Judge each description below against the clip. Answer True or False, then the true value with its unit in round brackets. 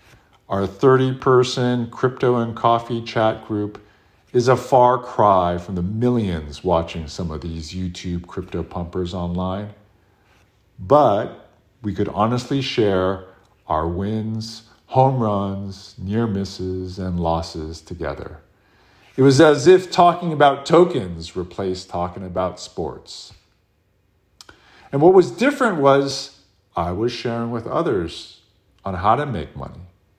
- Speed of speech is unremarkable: False (125 wpm)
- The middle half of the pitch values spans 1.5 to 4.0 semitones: False (5.1 semitones)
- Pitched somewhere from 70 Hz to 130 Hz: True (100 Hz)